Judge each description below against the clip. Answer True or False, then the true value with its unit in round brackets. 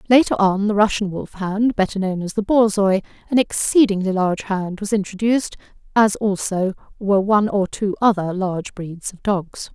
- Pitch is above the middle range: True (200 Hz)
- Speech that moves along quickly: False (165 wpm)